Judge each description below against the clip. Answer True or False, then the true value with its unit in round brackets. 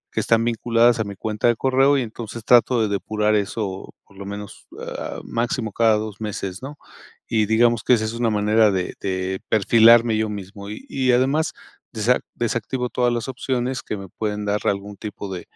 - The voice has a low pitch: True (110 Hz)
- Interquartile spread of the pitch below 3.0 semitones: True (2.5 semitones)